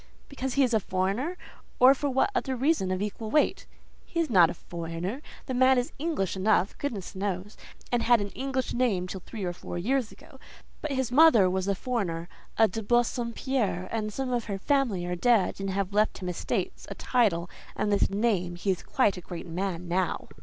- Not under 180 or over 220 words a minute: Yes, fast, 205 wpm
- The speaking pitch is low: No, high, 210 Hz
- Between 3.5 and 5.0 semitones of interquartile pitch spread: No, wide, 5.5 semitones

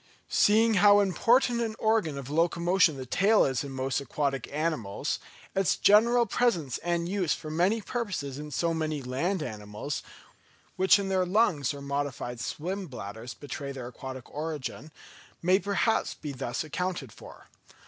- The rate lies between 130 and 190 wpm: Yes, average, 150 wpm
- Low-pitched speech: No, medium, 160 Hz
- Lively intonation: Yes, wide, 6.1 semitones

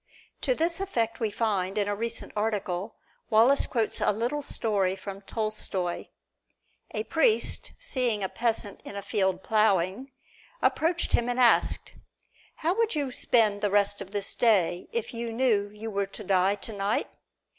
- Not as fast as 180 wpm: Yes, average, 155 wpm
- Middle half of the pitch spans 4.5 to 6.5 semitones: No, average, 3.3 semitones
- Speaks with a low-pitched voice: No, high, 215 Hz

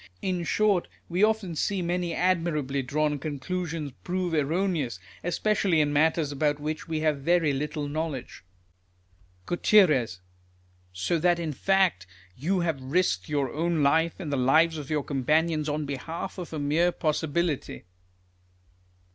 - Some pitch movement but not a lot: Yes, average, 3.2 semitones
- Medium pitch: Yes, medium, 160 Hz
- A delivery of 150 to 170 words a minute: No, average, 140 wpm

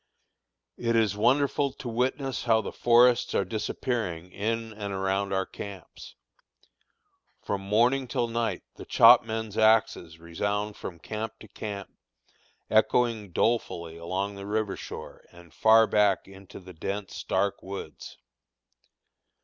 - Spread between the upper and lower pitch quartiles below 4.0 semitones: Yes, average, 2.9 semitones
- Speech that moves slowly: Yes, slow, 125 wpm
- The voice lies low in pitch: Yes, low, 105 Hz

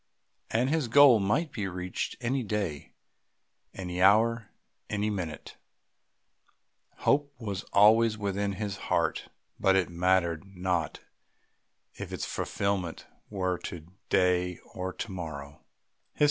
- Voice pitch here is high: No, very low, 95 Hz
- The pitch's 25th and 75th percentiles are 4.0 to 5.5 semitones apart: No, average, 3.2 semitones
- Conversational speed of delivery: No, slow, 115 wpm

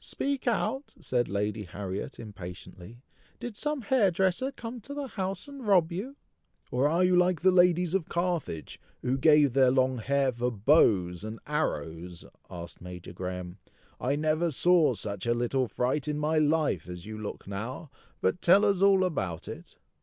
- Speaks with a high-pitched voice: No, medium, 145 Hz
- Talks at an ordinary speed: Yes, average, 170 wpm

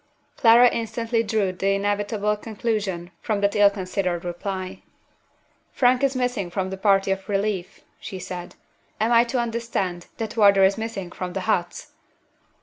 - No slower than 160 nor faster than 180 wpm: No, average, 150 wpm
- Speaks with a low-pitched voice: No, high, 200 Hz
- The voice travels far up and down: No, average, 3.2 semitones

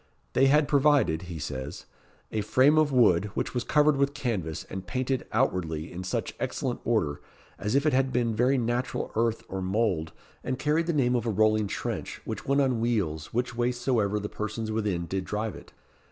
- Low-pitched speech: Yes, low, 115 Hz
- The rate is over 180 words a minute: Yes, average, 195 wpm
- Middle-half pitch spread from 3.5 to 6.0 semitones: Yes, wide, 5.6 semitones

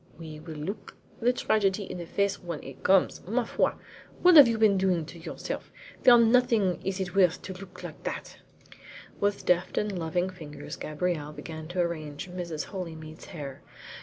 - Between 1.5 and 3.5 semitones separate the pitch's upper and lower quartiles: No, average, 3.9 semitones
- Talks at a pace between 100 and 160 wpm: No, average, 175 wpm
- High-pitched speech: No, medium, 180 Hz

